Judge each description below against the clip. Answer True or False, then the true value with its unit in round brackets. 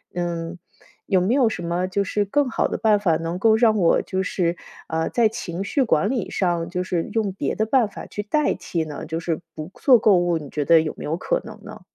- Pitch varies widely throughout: False (4.5 semitones)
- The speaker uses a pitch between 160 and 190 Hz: True (185 Hz)